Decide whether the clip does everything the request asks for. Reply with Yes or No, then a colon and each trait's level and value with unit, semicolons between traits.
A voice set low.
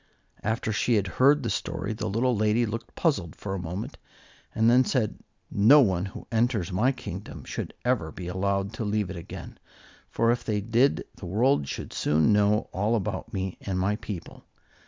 Yes: low, 105 Hz